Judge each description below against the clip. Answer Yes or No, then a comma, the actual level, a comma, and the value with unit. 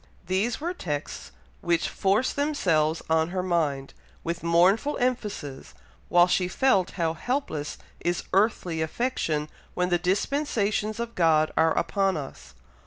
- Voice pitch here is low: No, medium, 180 Hz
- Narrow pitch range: No, average, 5.2 semitones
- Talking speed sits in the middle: No, slow, 130 wpm